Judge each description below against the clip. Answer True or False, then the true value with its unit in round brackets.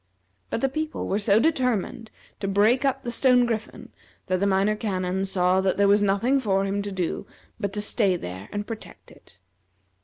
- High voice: True (205 Hz)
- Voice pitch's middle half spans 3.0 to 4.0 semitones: True (3.7 semitones)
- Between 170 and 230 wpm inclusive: True (190 wpm)